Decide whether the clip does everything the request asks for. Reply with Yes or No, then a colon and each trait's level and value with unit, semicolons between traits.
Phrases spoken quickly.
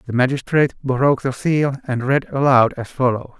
No: average, 175 wpm